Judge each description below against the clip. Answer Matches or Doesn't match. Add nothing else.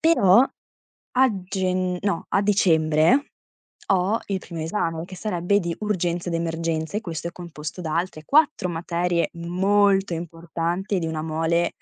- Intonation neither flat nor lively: Matches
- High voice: Doesn't match